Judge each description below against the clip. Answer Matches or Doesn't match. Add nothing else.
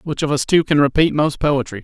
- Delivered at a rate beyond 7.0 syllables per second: Doesn't match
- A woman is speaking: Doesn't match